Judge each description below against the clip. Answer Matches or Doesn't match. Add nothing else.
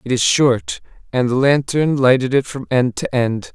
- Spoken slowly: Doesn't match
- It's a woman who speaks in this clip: Doesn't match